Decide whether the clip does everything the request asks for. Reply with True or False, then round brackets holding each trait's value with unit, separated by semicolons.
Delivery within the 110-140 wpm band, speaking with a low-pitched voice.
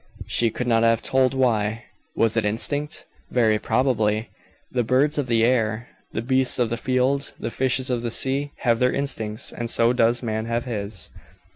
False (180 wpm; 120 Hz)